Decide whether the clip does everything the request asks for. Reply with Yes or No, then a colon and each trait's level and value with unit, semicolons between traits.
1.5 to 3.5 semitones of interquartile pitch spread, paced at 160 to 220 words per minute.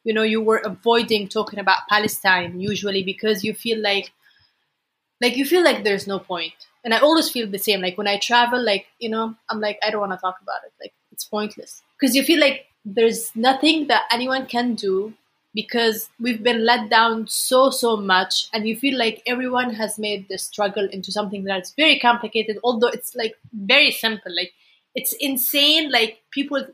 Yes: average, 3.2 semitones; average, 195 wpm